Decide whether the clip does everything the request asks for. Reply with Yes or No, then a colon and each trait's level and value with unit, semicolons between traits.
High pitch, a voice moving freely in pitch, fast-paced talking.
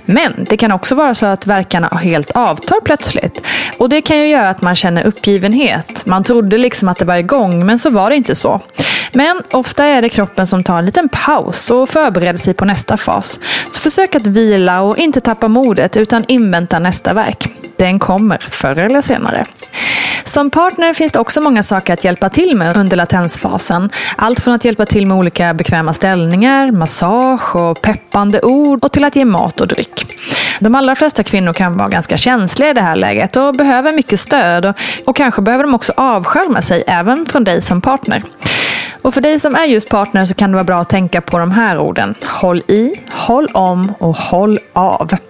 Yes: high, 215 Hz; wide, 6.2 semitones; fast, 200 wpm